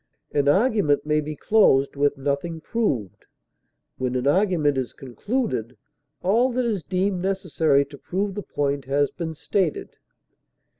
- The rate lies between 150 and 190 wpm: No, average, 140 wpm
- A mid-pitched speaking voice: Yes, medium, 155 Hz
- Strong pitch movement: Yes, wide, 5.8 semitones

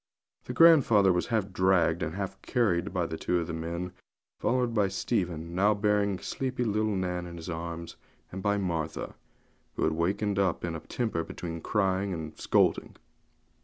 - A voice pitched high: No, very low, 95 Hz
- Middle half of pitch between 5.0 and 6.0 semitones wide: No, average, 3.4 semitones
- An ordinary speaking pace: Yes, average, 165 wpm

